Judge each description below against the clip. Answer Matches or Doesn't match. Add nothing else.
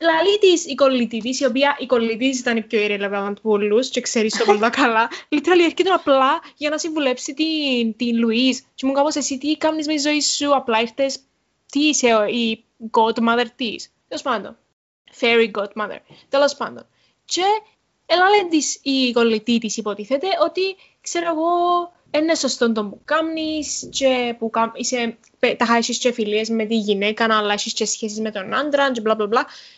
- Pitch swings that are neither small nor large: Matches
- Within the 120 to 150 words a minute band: Doesn't match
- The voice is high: Matches